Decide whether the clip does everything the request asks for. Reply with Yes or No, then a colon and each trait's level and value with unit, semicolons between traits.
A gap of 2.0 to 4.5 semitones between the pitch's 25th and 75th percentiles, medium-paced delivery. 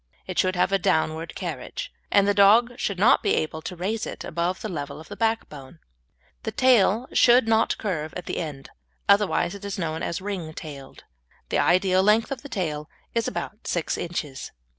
No: average, 5.0 semitones; average, 185 wpm